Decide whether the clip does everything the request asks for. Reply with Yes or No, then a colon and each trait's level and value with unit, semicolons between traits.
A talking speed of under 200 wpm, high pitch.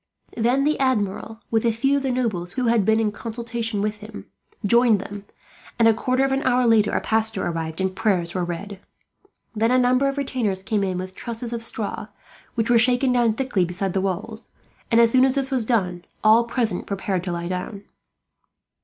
No: fast, 205 wpm; high, 225 Hz